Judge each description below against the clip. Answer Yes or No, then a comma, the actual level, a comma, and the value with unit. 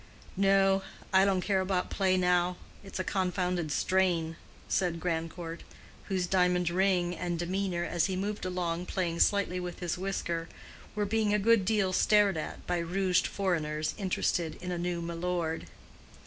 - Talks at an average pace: Yes, average, 155 wpm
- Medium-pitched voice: Yes, medium, 180 Hz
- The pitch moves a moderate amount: No, narrow, 2.0 semitones